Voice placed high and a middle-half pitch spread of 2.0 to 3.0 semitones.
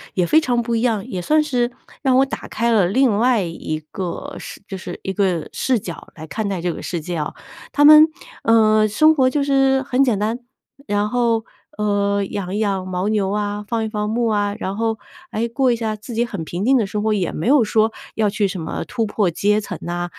No: high, 215 Hz; average, 3.6 semitones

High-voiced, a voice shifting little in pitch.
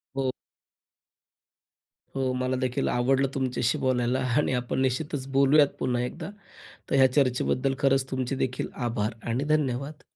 No: low, 130 Hz; narrow, 1.5 semitones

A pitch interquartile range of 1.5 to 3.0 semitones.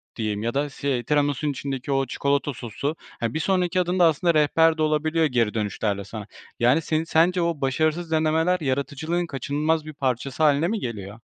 No: average, 3.9 semitones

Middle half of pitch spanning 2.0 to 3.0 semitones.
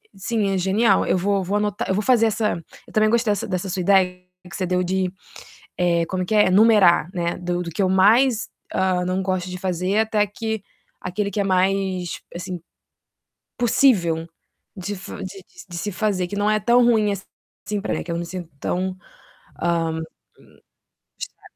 Yes: narrow, 2.5 semitones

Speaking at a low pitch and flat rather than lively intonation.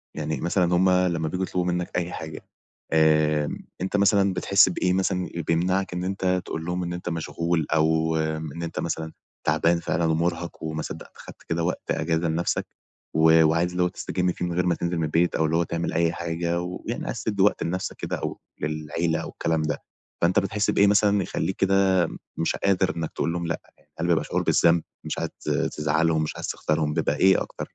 Yes: very low, 85 Hz; narrow, 2.2 semitones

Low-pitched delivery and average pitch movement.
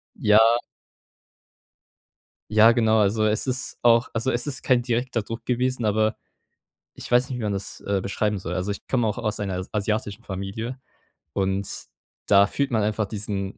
Yes: low, 110 Hz; average, 3.0 semitones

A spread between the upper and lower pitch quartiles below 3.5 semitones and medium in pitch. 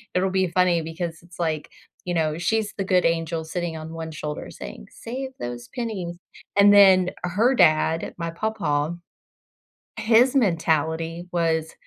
Yes: average, 3.1 semitones; medium, 170 Hz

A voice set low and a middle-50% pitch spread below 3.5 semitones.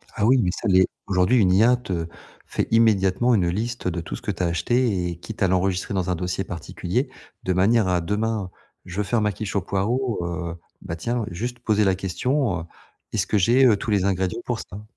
No: low, 100 Hz; average, 3.9 semitones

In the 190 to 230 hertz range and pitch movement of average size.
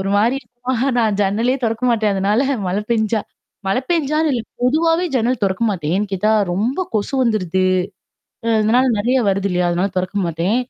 Yes: high, 215 Hz; average, 4.3 semitones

